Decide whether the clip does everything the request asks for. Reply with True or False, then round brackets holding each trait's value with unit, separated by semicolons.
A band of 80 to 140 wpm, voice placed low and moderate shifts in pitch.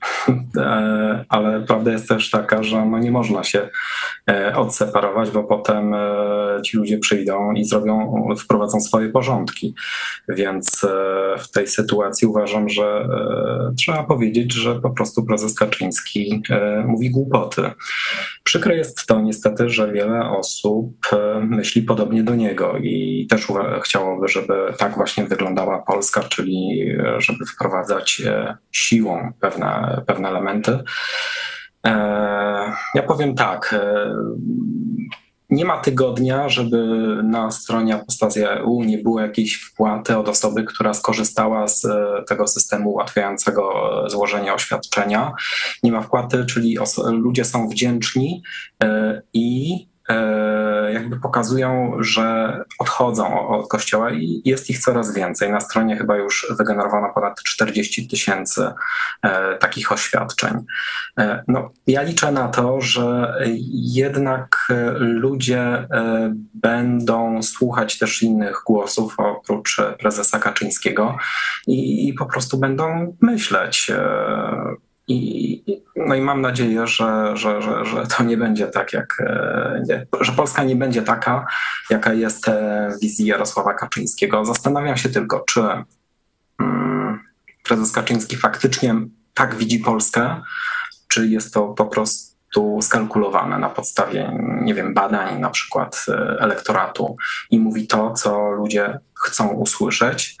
True (115 wpm; 110 Hz; 3.0 semitones)